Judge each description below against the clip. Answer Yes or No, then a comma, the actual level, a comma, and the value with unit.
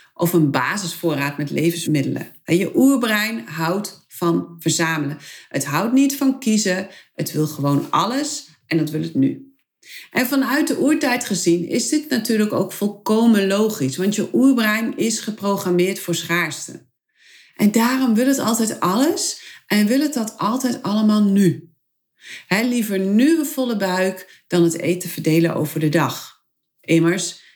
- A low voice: No, high, 200 Hz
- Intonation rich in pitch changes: Yes, wide, 6.9 semitones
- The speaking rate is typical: Yes, average, 150 wpm